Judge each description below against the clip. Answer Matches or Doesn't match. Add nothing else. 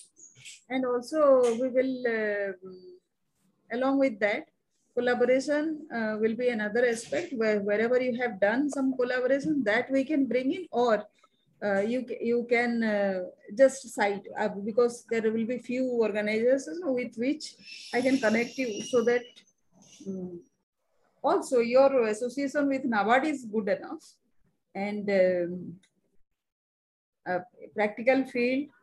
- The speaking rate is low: Matches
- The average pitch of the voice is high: Matches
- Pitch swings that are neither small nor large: Matches